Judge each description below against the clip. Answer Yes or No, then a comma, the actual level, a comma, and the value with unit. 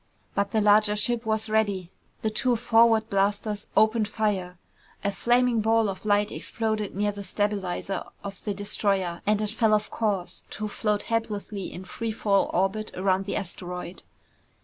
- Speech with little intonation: Yes, narrow, 1.9 semitones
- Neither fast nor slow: Yes, average, 160 wpm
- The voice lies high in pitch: Yes, high, 210 Hz